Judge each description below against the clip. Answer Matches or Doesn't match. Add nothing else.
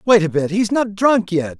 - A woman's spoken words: Doesn't match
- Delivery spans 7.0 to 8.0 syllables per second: Doesn't match